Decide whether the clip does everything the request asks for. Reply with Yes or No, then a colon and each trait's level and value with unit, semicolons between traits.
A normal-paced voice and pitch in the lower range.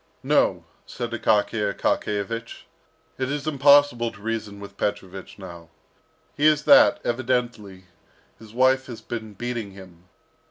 No: slow, 125 wpm; low, 115 Hz